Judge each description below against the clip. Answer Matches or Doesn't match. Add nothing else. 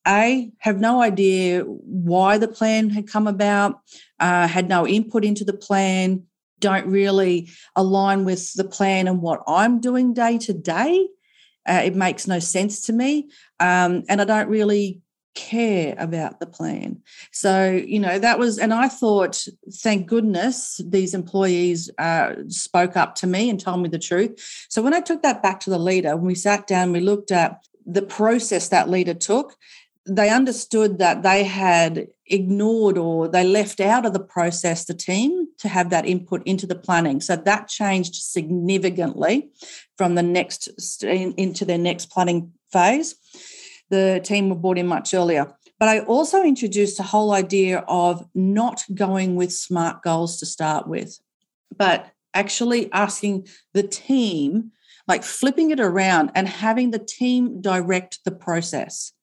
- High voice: Matches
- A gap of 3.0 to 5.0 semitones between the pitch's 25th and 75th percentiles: Matches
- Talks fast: Doesn't match